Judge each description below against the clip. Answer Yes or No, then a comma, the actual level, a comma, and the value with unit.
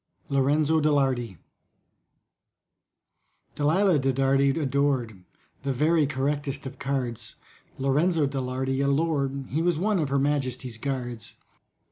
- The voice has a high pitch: No, medium, 140 Hz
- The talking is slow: Yes, slow, 120 wpm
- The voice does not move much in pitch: Yes, narrow, 2.0 semitones